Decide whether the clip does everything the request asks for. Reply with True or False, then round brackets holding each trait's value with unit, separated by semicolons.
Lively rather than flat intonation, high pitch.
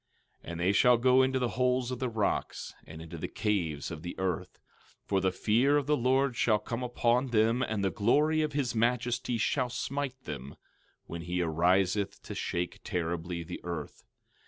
False (6.2 semitones; 110 Hz)